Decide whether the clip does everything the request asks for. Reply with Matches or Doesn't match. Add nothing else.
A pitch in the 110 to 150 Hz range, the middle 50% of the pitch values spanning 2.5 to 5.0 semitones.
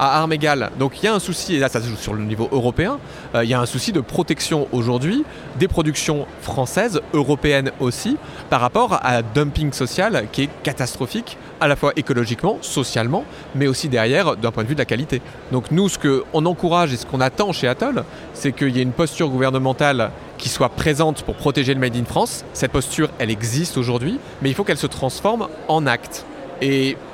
Matches